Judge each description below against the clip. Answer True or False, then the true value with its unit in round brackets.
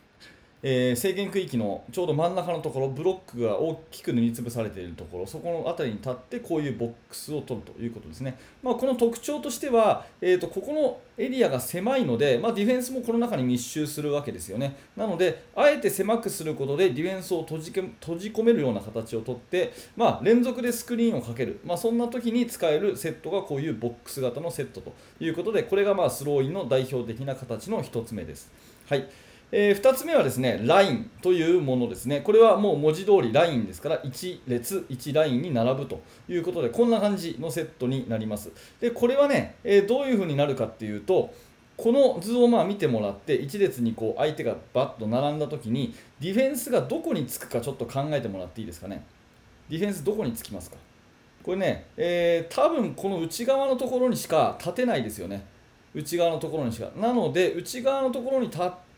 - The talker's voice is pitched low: False (165 Hz)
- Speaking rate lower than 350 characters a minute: False (430 characters per minute)